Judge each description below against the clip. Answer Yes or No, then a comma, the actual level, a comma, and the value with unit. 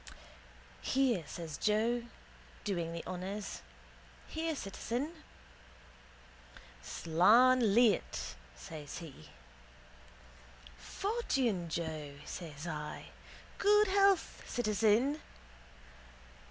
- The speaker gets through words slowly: Yes, slow, 70 wpm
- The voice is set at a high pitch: Yes, high, 210 Hz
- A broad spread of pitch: Yes, wide, 7.6 semitones